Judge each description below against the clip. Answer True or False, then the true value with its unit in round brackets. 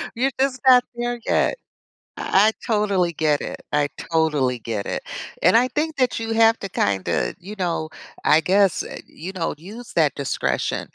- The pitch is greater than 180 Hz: True (190 Hz)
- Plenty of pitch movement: True (7.2 semitones)